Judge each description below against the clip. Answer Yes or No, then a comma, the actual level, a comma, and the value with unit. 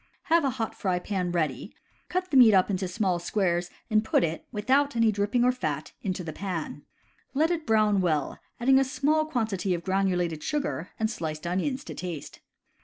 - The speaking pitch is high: Yes, high, 200 Hz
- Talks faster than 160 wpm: Yes, average, 185 wpm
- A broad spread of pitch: Yes, wide, 6.3 semitones